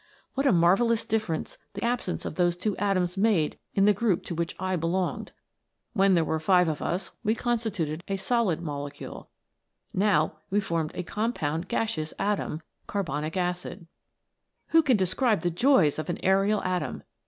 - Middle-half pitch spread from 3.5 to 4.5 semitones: Yes, average, 4.1 semitones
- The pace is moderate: Yes, average, 165 wpm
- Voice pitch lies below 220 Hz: Yes, medium, 185 Hz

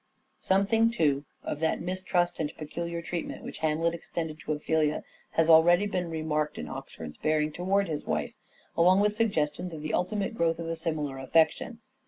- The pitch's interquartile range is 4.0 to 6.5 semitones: No, average, 3.0 semitones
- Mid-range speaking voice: Yes, medium, 165 Hz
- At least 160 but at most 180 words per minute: Yes, average, 170 wpm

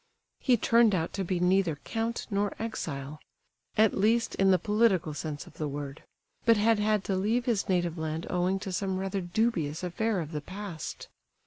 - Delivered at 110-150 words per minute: No, average, 175 wpm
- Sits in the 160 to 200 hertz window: Yes, high, 190 Hz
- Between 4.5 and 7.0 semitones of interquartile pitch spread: Yes, average, 5.0 semitones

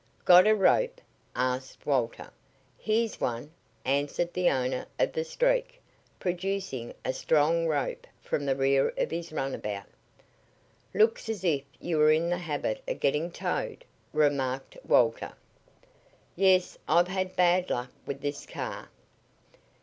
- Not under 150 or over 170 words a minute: No, slow, 135 wpm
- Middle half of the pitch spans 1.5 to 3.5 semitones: No, wide, 5.5 semitones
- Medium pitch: Yes, medium, 160 Hz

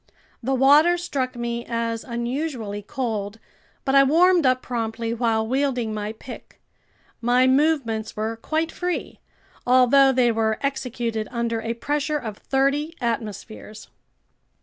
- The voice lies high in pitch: Yes, high, 245 Hz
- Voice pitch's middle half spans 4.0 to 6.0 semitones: No, average, 3.5 semitones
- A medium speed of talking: No, slow, 125 wpm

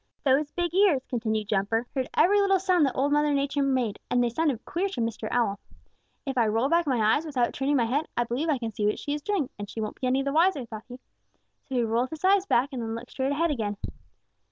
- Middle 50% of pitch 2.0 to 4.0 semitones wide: No, average, 4.6 semitones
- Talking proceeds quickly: Yes, fast, 250 wpm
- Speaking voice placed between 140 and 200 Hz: No, very high, 265 Hz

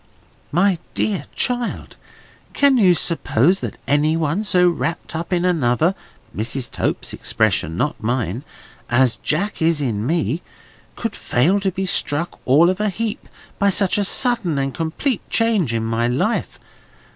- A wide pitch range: Yes, wide, 6.5 semitones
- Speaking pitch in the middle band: Yes, medium, 170 Hz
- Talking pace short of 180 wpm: Yes, average, 145 wpm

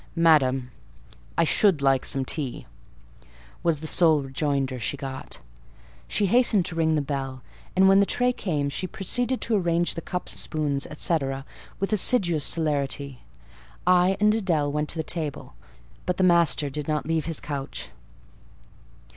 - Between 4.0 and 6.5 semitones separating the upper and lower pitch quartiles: Yes, average, 4.4 semitones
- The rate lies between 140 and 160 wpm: Yes, average, 155 wpm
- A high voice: No, medium, 160 Hz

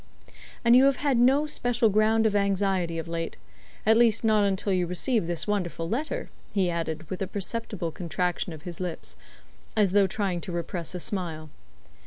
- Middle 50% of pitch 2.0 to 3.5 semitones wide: No, average, 4.4 semitones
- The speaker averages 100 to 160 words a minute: No, average, 180 wpm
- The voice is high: Yes, high, 195 Hz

